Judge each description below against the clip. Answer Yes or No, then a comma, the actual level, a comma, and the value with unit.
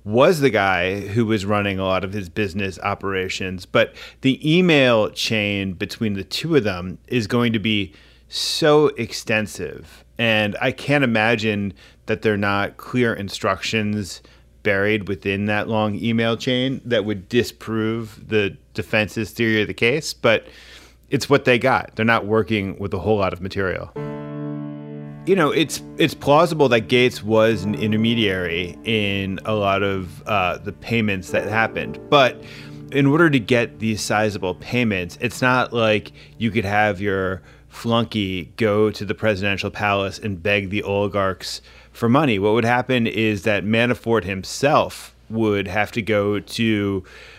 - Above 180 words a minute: No, average, 155 wpm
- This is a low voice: Yes, low, 105 Hz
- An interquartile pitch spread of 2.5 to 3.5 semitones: Yes, average, 2.8 semitones